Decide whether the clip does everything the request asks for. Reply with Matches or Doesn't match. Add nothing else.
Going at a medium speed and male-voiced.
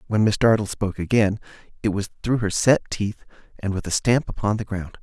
Doesn't match